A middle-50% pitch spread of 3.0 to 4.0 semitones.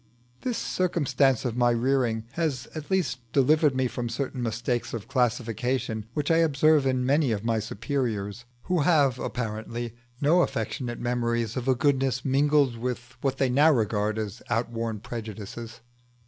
Yes: average, 3.4 semitones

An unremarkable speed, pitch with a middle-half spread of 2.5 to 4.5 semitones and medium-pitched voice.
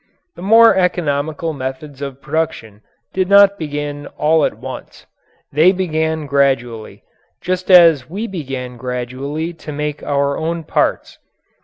No: slow, 130 wpm; average, 3.7 semitones; medium, 150 Hz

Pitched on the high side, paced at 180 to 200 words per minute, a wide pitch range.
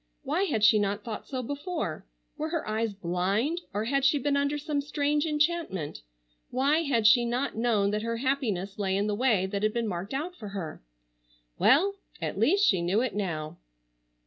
Yes: high, 230 Hz; average, 190 wpm; wide, 6.1 semitones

